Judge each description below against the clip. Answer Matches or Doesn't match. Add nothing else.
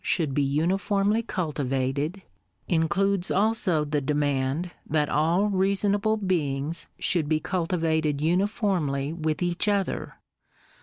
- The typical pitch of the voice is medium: Matches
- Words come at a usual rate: Doesn't match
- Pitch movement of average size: Matches